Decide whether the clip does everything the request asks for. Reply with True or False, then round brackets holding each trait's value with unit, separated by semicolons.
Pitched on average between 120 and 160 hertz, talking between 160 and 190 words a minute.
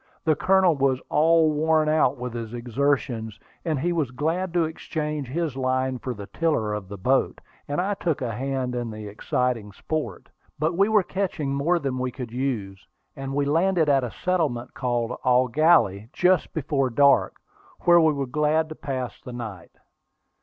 True (140 Hz; 180 wpm)